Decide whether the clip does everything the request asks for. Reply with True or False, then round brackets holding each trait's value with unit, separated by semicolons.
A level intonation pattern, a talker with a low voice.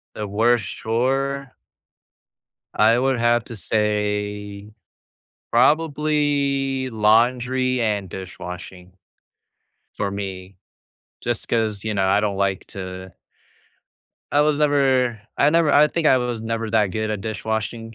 False (4.2 semitones; 115 Hz)